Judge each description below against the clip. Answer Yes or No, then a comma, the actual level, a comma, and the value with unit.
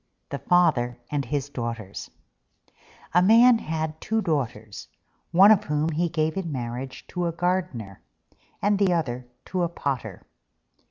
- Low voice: No, medium, 155 Hz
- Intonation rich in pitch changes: Yes, wide, 6.3 semitones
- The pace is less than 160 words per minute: Yes, average, 145 wpm